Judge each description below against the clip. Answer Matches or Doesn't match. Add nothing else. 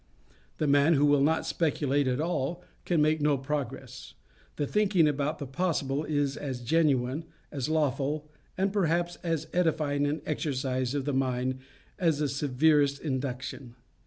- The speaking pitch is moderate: Matches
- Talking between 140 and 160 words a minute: Matches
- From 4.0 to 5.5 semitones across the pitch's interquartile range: Doesn't match